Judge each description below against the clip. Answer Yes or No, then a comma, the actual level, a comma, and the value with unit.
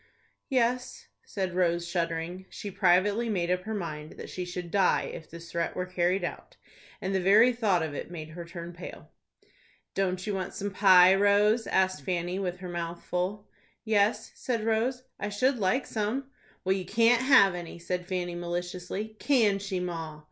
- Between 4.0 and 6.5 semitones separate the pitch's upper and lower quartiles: No, average, 3.0 semitones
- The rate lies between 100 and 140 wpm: No, average, 175 wpm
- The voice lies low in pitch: No, medium, 185 Hz